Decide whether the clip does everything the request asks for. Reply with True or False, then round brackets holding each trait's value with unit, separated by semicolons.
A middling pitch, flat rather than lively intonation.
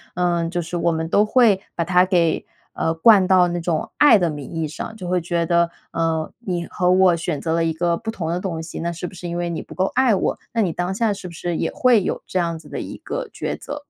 True (175 Hz; 2.2 semitones)